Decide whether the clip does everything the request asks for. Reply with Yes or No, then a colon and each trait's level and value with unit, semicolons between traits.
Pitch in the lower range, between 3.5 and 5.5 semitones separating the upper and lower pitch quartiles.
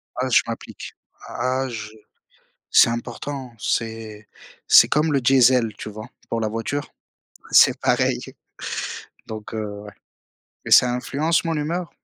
Yes: low, 120 Hz; average, 4.1 semitones